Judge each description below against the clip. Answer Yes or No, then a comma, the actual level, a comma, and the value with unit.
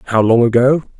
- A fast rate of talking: No, average, 180 wpm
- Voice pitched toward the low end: Yes, low, 120 Hz